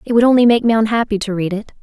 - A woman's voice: Yes, female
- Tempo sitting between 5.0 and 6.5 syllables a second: No, 7.4 syllables/s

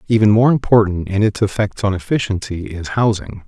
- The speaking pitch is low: Yes, low, 100 Hz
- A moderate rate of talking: Yes, average, 175 wpm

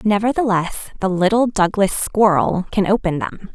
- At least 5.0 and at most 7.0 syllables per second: No, 4.8 syllables/s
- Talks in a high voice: Yes, high, 200 Hz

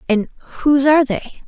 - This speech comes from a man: No, female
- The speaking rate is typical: Yes, average, 165 wpm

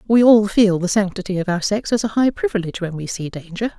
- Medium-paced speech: No, fast, 255 wpm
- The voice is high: Yes, high, 200 Hz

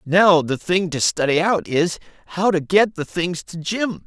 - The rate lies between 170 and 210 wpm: Yes, fast, 205 wpm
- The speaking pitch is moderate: Yes, medium, 175 Hz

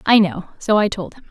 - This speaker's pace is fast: Yes, fast, 275 wpm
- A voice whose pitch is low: No, high, 210 Hz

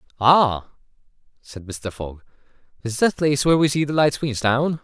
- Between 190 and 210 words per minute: No, average, 160 wpm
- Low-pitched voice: Yes, low, 130 Hz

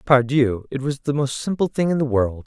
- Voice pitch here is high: No, low, 135 Hz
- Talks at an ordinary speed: No, fast, 245 wpm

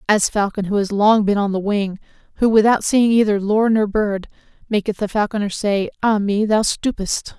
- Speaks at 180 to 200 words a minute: Yes, average, 195 wpm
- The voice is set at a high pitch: Yes, high, 210 Hz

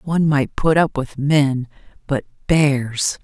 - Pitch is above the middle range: No, medium, 145 Hz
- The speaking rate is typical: Yes, average, 150 wpm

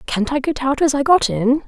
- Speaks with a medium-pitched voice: No, very high, 275 Hz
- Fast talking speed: Yes, fast, 285 wpm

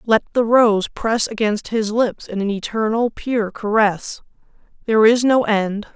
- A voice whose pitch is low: No, high, 220 Hz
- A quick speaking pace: No, average, 160 wpm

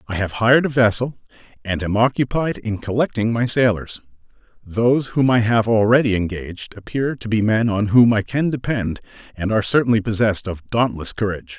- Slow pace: No, average, 175 wpm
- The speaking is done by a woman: No, male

